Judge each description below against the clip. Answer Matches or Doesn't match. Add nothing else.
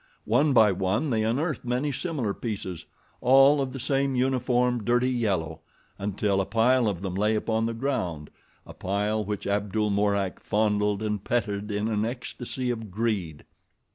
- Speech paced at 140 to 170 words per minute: Matches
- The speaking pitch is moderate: Doesn't match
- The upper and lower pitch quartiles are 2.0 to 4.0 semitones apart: Matches